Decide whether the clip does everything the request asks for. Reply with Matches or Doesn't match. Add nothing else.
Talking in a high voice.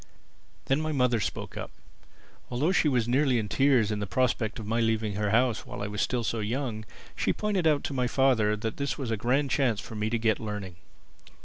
Doesn't match